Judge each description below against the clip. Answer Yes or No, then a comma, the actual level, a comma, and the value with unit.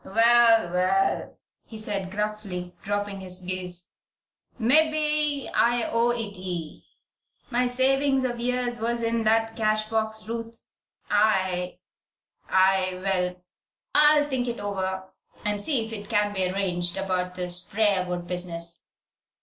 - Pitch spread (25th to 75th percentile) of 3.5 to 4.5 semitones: Yes, average, 4.1 semitones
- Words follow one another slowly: Yes, slow, 125 wpm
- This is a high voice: Yes, high, 210 Hz